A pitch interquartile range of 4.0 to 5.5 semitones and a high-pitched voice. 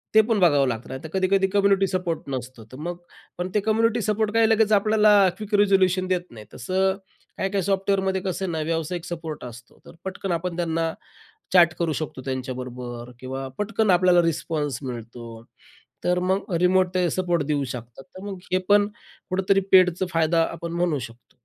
No: average, 5.0 semitones; medium, 175 Hz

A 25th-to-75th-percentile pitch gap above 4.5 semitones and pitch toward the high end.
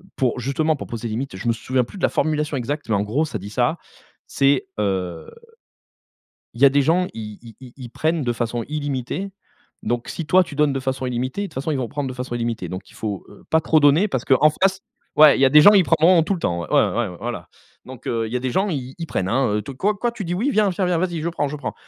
No: average, 5.1 semitones; low, 135 Hz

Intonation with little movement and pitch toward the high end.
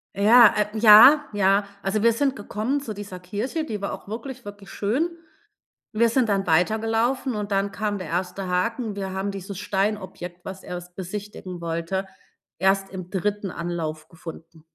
No: average, 3.0 semitones; high, 200 Hz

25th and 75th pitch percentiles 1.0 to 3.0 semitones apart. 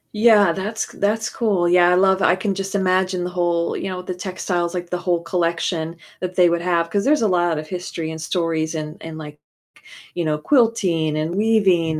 Yes: narrow, 2.4 semitones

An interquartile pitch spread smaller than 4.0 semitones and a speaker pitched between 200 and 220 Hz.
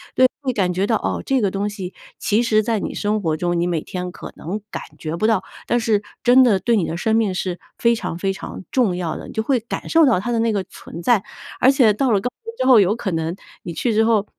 No: average, 4.3 semitones; high, 210 Hz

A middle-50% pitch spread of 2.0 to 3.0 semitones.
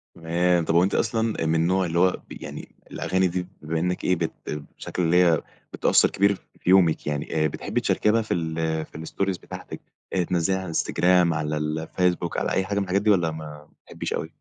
Yes: narrow, 2.6 semitones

